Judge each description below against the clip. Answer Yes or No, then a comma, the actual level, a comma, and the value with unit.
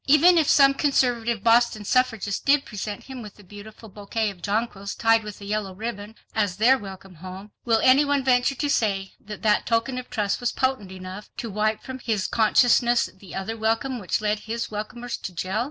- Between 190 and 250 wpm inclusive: Yes, average, 200 wpm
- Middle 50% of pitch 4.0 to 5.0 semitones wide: No, average, 3.2 semitones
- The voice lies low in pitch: No, high, 220 Hz